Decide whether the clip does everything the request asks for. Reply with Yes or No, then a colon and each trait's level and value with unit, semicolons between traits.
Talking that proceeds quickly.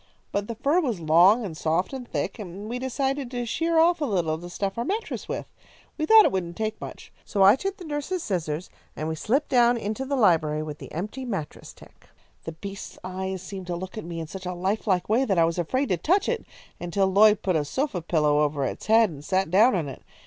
Yes: fast, 240 wpm